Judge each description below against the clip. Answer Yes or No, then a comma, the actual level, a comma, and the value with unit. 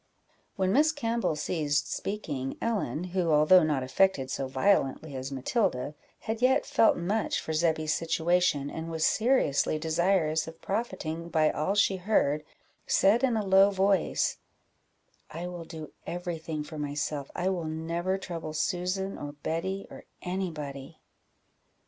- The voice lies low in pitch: No, medium, 170 Hz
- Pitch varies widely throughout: No, average, 4.0 semitones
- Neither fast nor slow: Yes, average, 150 wpm